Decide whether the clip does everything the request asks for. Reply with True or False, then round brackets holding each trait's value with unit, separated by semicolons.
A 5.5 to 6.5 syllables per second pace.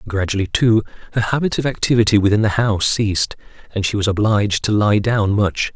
True (5.9 syllables/s)